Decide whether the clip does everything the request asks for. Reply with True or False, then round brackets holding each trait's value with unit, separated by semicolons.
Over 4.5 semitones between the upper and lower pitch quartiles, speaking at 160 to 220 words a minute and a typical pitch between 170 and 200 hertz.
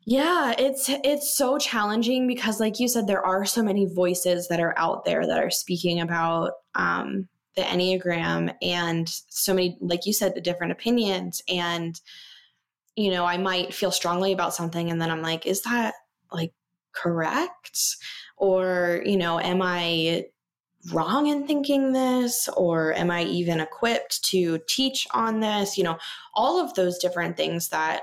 True (5.1 semitones; 165 wpm; 185 Hz)